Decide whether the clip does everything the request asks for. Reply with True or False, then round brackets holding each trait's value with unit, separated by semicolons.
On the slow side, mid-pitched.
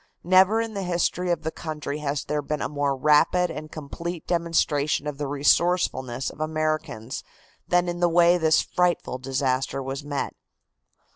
False (160 wpm; 155 Hz)